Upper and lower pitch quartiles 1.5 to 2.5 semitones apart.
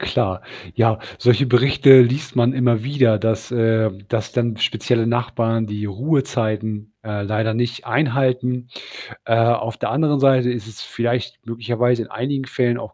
Yes: narrow, 2.1 semitones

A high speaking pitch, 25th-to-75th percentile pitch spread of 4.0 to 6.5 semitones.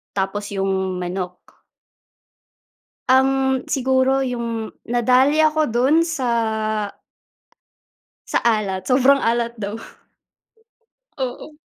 Yes: high, 245 Hz; average, 4.5 semitones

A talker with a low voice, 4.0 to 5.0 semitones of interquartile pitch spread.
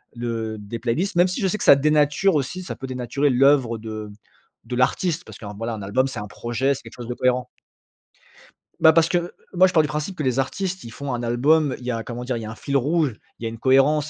Yes: low, 130 Hz; average, 4.5 semitones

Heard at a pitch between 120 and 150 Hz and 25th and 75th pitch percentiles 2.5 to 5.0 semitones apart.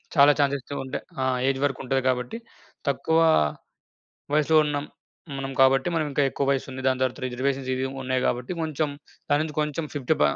No: low, 135 Hz; narrow, 2.1 semitones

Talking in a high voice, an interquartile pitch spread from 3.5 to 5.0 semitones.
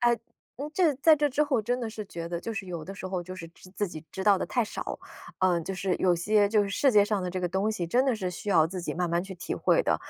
Yes: high, 195 Hz; average, 4.2 semitones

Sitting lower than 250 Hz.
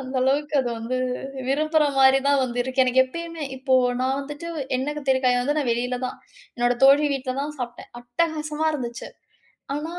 No: very high, 270 Hz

